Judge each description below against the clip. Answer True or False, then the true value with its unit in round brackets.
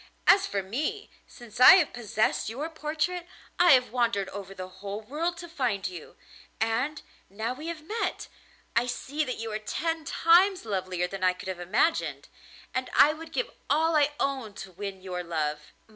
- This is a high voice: True (245 Hz)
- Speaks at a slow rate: False (180 wpm)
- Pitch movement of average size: False (8.1 semitones)